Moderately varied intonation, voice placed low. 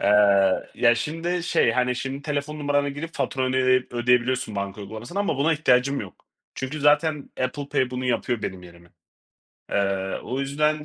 Yes: average, 3.7 semitones; low, 130 Hz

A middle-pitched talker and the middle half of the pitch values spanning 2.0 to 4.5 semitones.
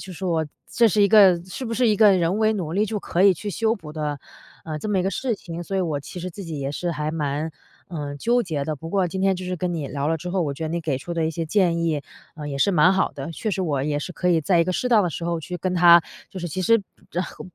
Yes: medium, 175 Hz; average, 3.6 semitones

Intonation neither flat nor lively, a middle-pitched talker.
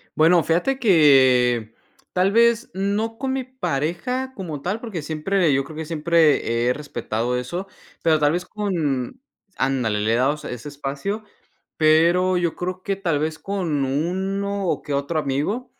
No: wide, 5.7 semitones; medium, 165 Hz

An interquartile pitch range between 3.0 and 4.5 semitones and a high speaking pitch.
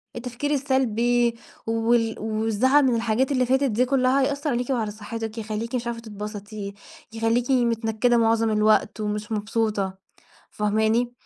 No: narrow, 2.4 semitones; high, 230 Hz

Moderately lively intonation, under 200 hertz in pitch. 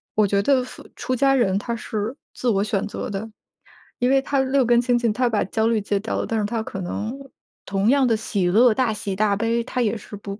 No: average, 3.3 semitones; high, 225 Hz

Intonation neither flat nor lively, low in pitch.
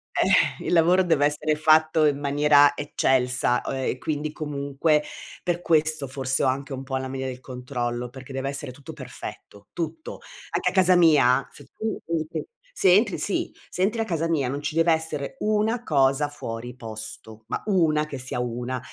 No: average, 3.7 semitones; medium, 145 Hz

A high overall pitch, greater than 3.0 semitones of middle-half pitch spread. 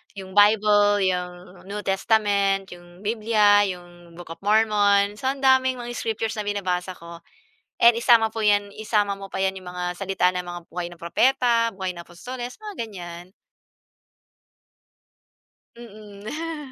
Yes: high, 205 Hz; average, 3.6 semitones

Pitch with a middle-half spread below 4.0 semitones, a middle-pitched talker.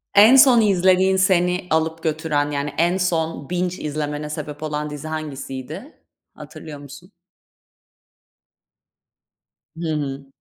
Yes: average, 3.6 semitones; medium, 160 Hz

